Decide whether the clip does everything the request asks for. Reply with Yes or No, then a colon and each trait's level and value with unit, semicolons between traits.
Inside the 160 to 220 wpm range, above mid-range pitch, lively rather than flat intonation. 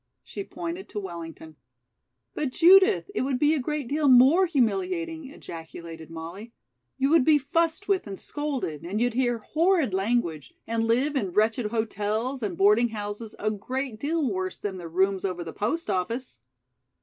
Yes: average, 165 wpm; high, 235 Hz; wide, 7.3 semitones